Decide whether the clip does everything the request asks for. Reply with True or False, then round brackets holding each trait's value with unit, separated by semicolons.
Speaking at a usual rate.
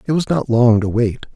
False (265 wpm)